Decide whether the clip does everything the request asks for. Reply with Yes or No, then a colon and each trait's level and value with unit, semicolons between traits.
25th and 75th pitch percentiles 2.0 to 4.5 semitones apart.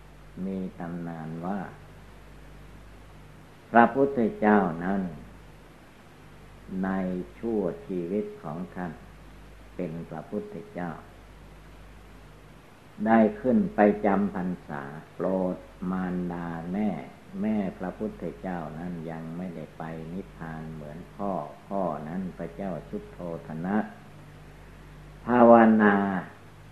Yes: average, 4.0 semitones